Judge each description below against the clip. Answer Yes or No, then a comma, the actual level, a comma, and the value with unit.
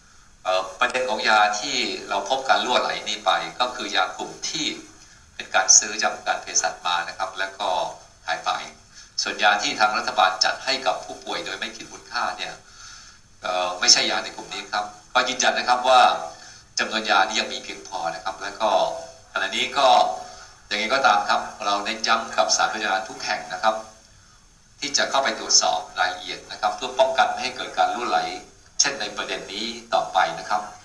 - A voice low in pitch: Yes, low, 105 Hz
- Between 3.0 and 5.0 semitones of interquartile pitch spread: Yes, average, 4.7 semitones